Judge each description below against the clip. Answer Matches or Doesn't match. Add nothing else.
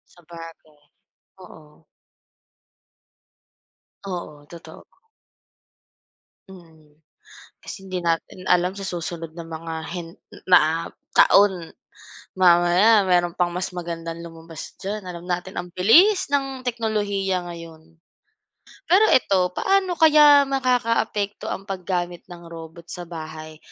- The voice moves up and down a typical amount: Matches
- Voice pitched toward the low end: Doesn't match